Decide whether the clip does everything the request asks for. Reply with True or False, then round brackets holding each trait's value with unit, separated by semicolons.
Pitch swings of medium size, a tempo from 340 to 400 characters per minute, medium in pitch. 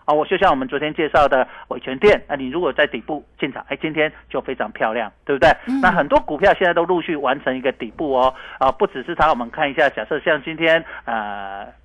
True (4.8 semitones; 350 characters per minute; 155 Hz)